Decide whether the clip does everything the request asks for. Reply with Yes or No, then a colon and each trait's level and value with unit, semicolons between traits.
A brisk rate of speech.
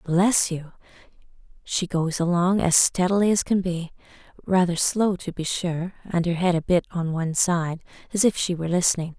No: average, 190 wpm